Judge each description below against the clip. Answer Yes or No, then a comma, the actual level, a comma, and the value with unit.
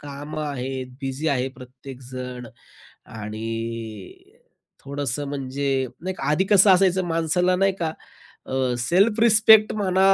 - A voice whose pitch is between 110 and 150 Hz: Yes, medium, 140 Hz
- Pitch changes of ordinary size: No, wide, 6.5 semitones